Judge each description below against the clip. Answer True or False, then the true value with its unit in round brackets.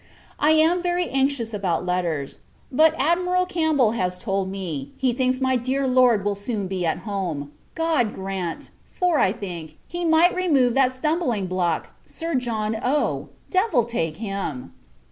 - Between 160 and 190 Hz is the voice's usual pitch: False (240 Hz)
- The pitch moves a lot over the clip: True (8.3 semitones)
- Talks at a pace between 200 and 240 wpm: False (155 wpm)